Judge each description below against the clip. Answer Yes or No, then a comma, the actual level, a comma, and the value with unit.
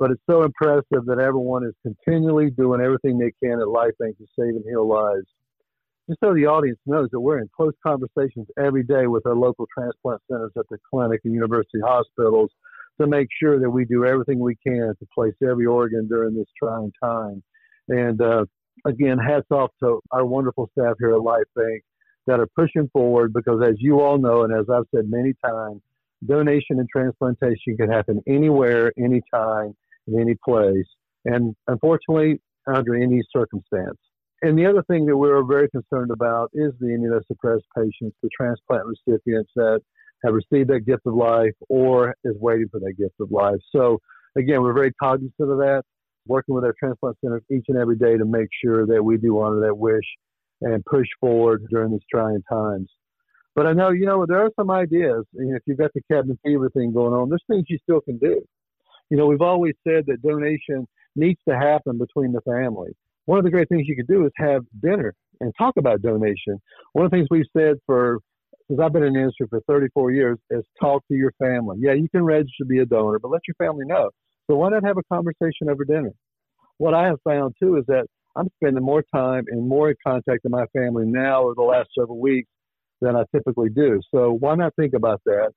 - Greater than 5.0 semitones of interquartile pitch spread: No, average, 4.1 semitones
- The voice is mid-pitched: No, low, 130 Hz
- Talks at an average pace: No, fast, 210 wpm